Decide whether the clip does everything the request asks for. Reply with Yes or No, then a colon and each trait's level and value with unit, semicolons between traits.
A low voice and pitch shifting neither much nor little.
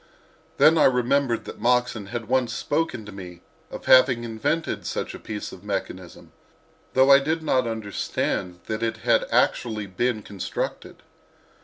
Yes: low, 115 Hz; average, 4.0 semitones